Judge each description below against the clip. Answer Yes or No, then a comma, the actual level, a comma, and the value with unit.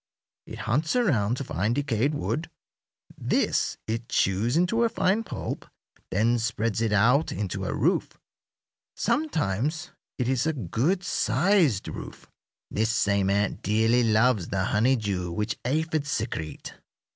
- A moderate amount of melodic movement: No, wide, 6.5 semitones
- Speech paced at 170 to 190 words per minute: No, slow, 135 wpm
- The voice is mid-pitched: No, low, 115 Hz